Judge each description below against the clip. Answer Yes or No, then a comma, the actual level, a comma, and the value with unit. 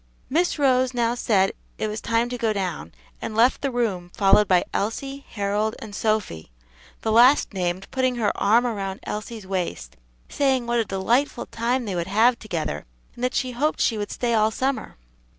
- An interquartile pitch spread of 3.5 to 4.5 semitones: Yes, average, 4.1 semitones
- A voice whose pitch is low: No, high, 220 Hz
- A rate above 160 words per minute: Yes, average, 185 wpm